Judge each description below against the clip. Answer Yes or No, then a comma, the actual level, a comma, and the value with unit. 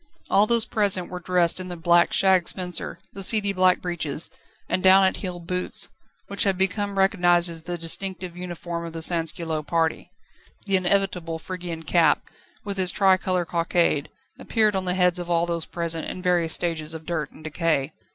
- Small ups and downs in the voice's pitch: Yes, narrow, 2.1 semitones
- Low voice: No, medium, 175 Hz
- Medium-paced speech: Yes, average, 180 wpm